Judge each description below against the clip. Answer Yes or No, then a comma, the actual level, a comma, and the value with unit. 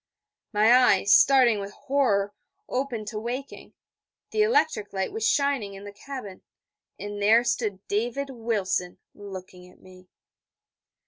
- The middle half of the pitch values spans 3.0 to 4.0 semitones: No, average, 4.5 semitones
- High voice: Yes, high, 215 Hz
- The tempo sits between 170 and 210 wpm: No, slow, 135 wpm